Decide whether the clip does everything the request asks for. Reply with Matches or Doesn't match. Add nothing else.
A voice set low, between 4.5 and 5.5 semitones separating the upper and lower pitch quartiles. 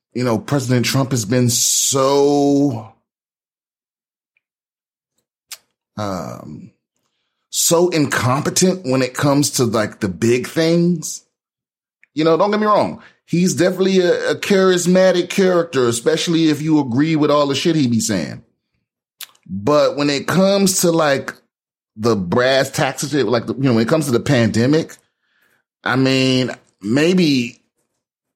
Doesn't match